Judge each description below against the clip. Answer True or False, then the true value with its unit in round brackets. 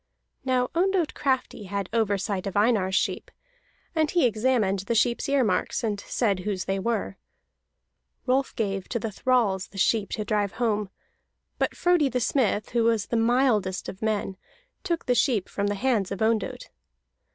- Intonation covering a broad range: False (4.1 semitones)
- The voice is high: True (220 Hz)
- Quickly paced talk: False (165 wpm)